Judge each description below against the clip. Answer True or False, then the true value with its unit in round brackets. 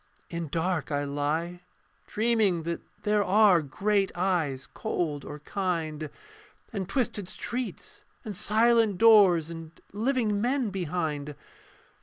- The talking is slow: True (115 wpm)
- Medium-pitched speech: True (180 Hz)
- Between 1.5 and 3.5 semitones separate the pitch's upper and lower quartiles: False (4.9 semitones)